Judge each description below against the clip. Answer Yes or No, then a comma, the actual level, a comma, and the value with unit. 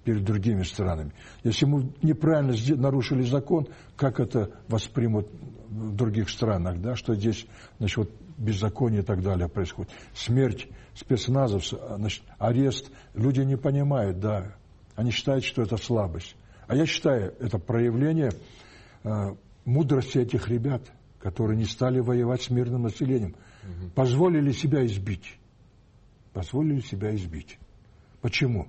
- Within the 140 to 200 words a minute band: No, average, 125 wpm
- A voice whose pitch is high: No, low, 115 Hz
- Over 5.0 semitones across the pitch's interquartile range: No, average, 4.0 semitones